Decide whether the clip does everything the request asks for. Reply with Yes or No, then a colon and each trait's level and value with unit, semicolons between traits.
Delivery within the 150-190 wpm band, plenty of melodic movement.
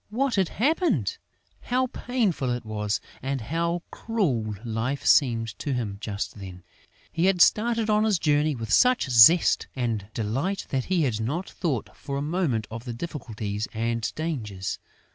Yes: average, 160 wpm; wide, 8.6 semitones